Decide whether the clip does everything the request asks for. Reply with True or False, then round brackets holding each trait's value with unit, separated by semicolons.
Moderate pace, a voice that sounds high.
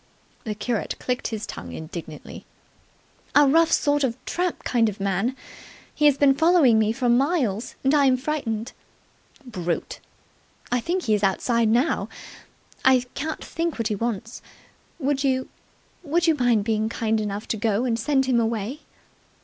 True (155 wpm; 245 Hz)